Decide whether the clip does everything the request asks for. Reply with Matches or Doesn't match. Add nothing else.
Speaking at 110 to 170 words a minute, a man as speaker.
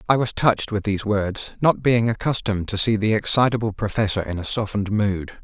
Doesn't match